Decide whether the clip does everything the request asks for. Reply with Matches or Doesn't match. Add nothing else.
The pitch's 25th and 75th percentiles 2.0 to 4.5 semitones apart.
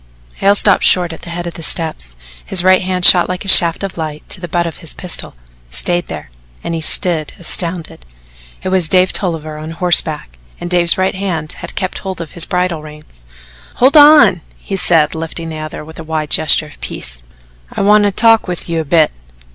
Matches